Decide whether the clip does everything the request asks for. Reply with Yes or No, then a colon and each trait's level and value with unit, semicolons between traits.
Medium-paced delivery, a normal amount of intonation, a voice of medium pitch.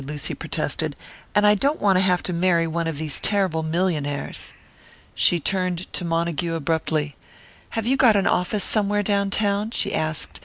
Yes: average, 170 wpm; average, 3.9 semitones; medium, 180 Hz